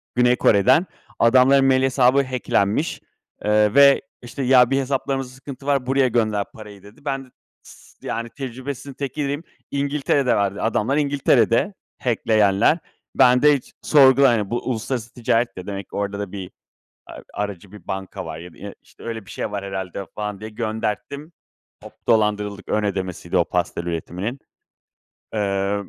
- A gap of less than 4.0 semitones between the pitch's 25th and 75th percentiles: No, average, 4.8 semitones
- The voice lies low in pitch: Yes, low, 115 Hz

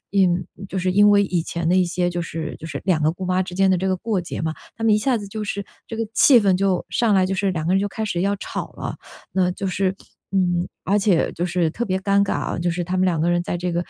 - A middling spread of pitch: No, narrow, 2.3 semitones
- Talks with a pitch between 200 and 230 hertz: No, medium, 185 Hz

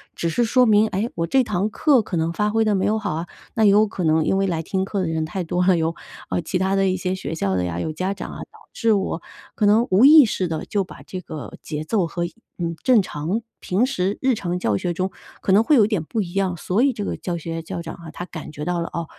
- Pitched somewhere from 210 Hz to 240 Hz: No, medium, 185 Hz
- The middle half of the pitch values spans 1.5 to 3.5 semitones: No, average, 4.1 semitones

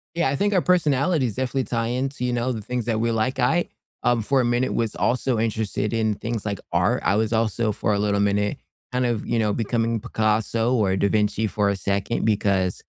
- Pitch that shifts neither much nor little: Yes, average, 3.0 semitones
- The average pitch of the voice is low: Yes, low, 115 Hz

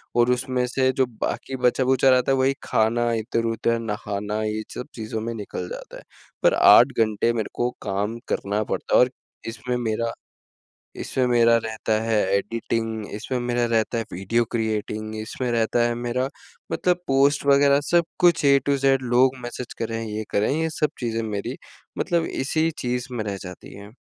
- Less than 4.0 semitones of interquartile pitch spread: Yes, average, 2.8 semitones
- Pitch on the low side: Yes, low, 120 Hz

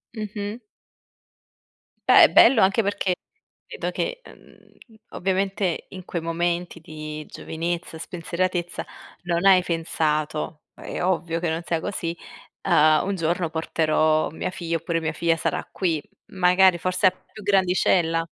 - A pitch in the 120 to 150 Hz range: No, medium, 175 Hz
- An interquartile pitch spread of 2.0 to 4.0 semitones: Yes, narrow, 2.4 semitones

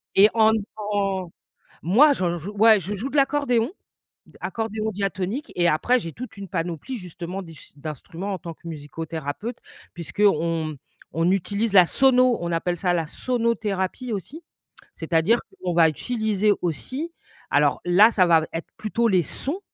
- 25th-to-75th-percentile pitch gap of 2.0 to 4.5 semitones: No, average, 5.1 semitones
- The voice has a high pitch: Yes, high, 195 Hz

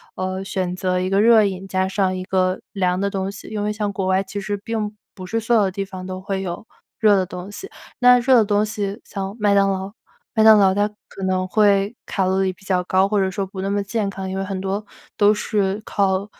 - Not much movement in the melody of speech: Yes, narrow, 1.6 semitones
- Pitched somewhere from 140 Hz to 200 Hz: Yes, high, 195 Hz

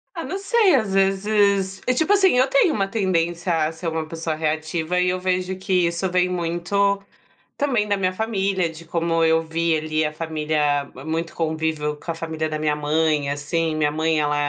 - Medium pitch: Yes, medium, 170 Hz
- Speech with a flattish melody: No, average, 3.5 semitones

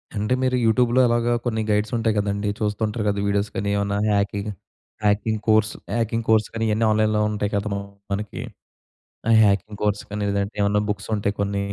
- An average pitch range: No, narrow, 1.5 semitones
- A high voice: No, low, 105 Hz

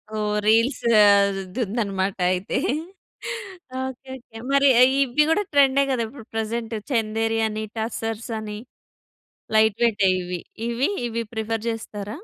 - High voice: Yes, high, 225 Hz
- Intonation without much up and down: Yes, narrow, 2.0 semitones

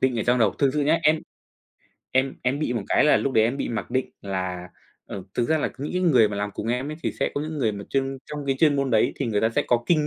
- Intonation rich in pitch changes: No, average, 4.6 semitones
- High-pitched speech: No, low, 130 Hz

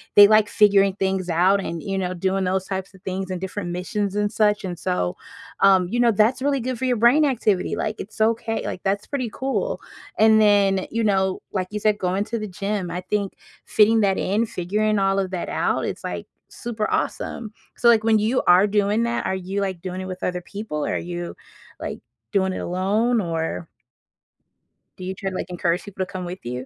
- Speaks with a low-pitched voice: No, high, 195 Hz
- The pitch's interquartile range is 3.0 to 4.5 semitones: No, narrow, 2.6 semitones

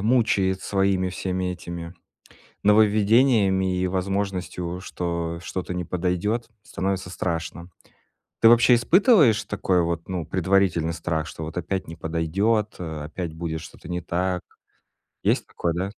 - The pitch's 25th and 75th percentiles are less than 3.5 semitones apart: Yes, average, 2.9 semitones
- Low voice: Yes, very low, 90 Hz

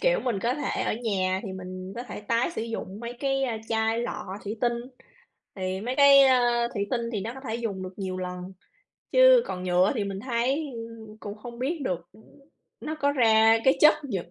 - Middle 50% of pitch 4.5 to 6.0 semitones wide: Yes, average, 5.3 semitones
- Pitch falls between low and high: No, high, 230 Hz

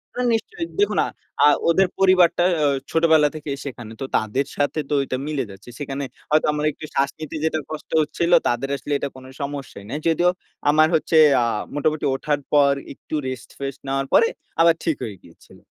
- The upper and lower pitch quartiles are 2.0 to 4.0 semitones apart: Yes, average, 2.7 semitones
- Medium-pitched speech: Yes, medium, 145 Hz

